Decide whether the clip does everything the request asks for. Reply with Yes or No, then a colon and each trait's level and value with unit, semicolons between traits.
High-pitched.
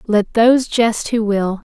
Yes: high, 220 Hz